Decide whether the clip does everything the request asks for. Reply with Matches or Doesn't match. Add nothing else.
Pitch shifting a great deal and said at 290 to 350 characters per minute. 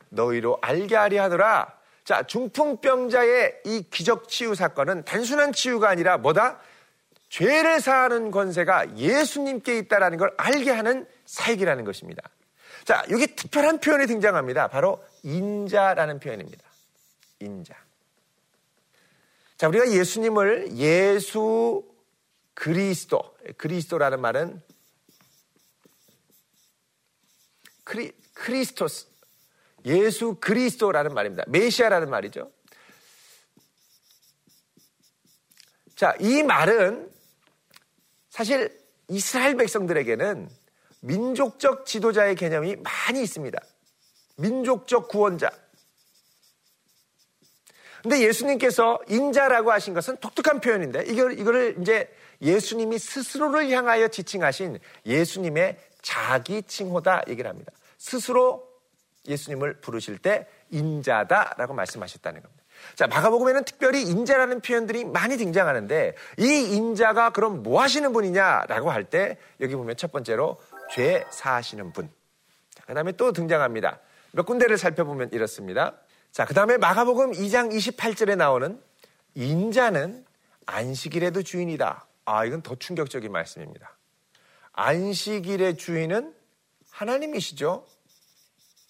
Doesn't match